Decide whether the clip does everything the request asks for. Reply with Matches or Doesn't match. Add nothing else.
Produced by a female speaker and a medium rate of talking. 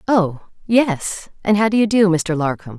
Matches